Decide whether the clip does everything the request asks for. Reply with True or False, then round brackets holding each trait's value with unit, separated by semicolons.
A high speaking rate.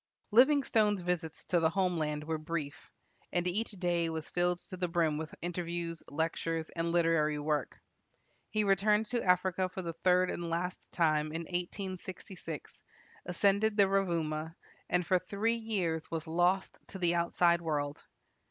False (150 wpm)